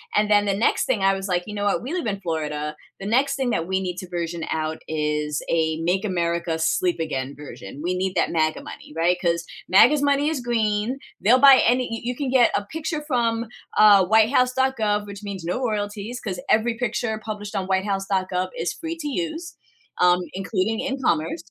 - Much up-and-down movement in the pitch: Yes, wide, 5.7 semitones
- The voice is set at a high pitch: Yes, high, 200 Hz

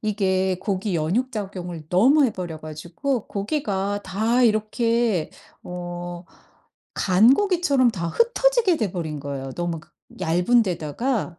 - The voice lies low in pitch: No, high, 195 Hz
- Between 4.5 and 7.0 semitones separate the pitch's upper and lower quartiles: Yes, average, 5.3 semitones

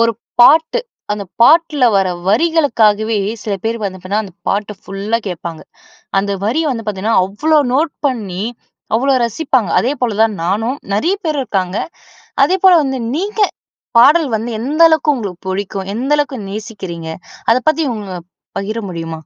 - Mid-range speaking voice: No, high, 225 Hz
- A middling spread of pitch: No, wide, 6.6 semitones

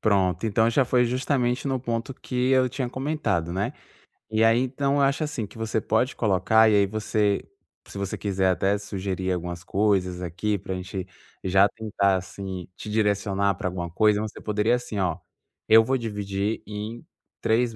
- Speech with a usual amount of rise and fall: Yes, average, 3.6 semitones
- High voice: No, low, 105 Hz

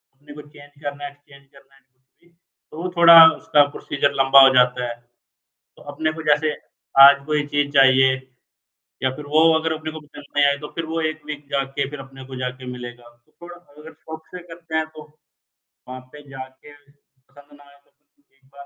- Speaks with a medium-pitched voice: Yes, medium, 145 Hz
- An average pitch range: No, narrow, 2.1 semitones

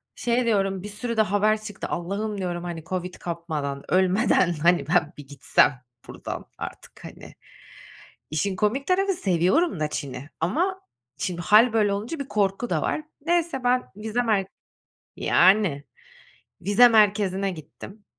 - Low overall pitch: No, high, 200 Hz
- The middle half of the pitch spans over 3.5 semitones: Yes, average, 4.6 semitones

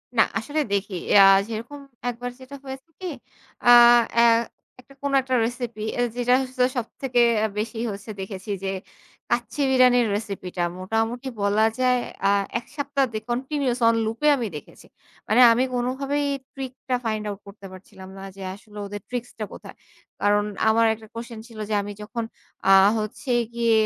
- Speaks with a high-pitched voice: Yes, high, 235 Hz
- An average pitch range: Yes, average, 3.1 semitones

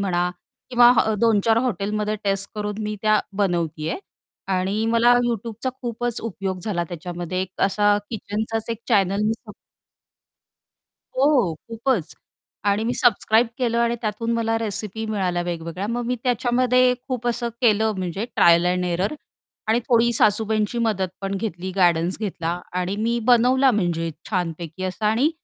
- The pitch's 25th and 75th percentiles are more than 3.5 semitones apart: Yes, average, 4.1 semitones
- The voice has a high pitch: Yes, high, 210 Hz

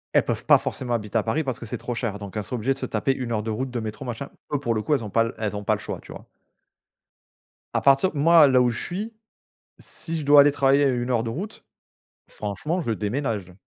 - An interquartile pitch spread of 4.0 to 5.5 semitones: Yes, average, 4.3 semitones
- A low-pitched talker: Yes, low, 120 Hz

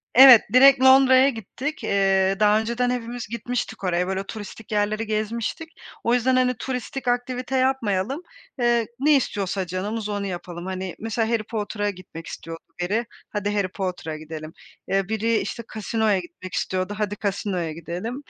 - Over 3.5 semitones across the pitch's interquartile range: Yes, average, 4.4 semitones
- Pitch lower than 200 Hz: No, high, 215 Hz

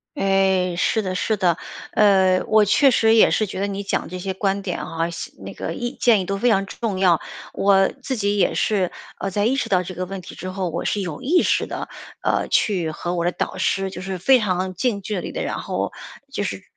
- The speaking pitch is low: No, high, 195 Hz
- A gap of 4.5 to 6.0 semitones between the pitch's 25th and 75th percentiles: No, narrow, 2.4 semitones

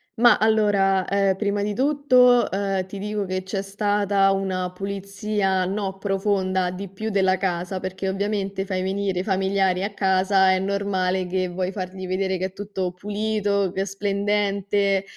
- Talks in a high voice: Yes, high, 195 Hz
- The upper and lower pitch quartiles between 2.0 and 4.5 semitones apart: No, narrow, 1.3 semitones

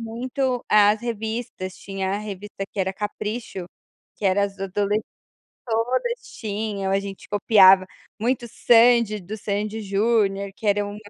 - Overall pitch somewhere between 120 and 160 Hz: No, high, 210 Hz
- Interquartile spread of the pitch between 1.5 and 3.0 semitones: Yes, narrow, 2.4 semitones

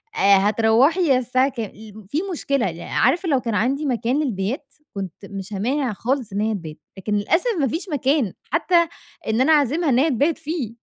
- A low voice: No, very high, 250 Hz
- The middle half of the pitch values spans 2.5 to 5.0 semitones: No, wide, 5.4 semitones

